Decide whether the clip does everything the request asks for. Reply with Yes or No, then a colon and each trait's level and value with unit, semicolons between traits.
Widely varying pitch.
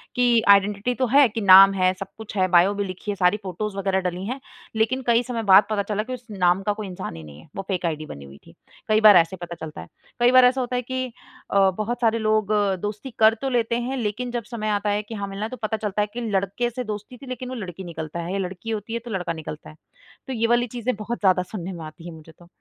No: average, 4.0 semitones